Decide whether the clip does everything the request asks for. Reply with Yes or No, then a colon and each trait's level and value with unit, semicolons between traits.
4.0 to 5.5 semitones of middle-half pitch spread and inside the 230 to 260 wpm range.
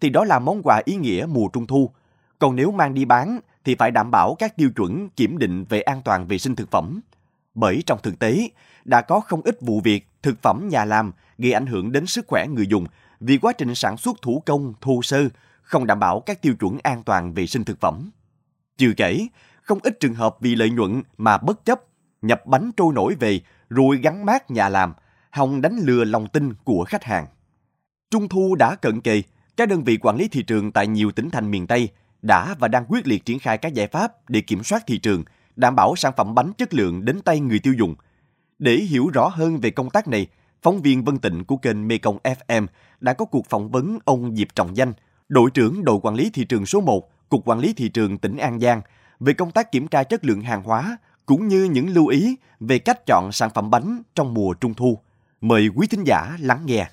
Yes: average, 5.1 semitones; average, 235 wpm